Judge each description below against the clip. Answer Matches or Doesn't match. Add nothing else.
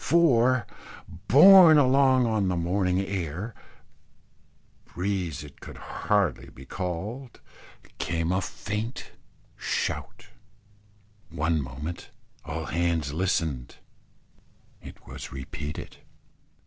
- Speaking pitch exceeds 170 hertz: Doesn't match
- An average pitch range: Doesn't match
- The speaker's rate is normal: Doesn't match